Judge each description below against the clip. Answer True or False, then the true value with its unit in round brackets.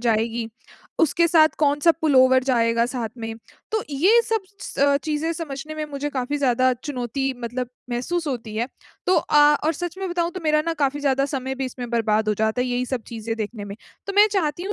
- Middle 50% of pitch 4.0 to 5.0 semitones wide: True (4.5 semitones)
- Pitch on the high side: True (270 Hz)